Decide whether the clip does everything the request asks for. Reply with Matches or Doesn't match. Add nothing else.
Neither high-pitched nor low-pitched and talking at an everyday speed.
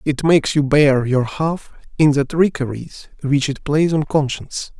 Matches